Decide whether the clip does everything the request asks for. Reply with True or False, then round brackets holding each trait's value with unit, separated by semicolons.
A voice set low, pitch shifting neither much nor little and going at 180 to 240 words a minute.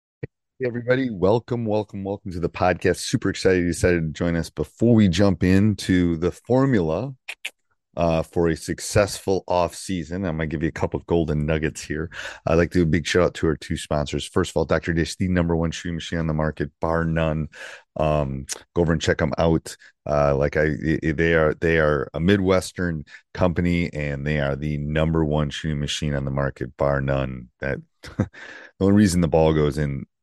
True (85 Hz; 3.0 semitones; 205 wpm)